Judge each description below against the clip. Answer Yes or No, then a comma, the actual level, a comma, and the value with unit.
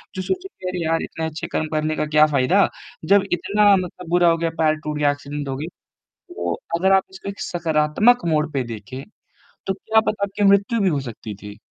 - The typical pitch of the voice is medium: Yes, medium, 165 Hz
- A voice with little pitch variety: No, average, 4.5 semitones